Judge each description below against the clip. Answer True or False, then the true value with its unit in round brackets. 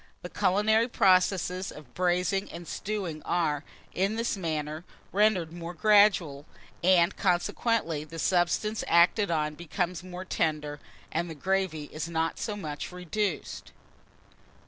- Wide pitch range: False (3.4 semitones)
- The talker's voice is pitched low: False (180 Hz)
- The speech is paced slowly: True (125 wpm)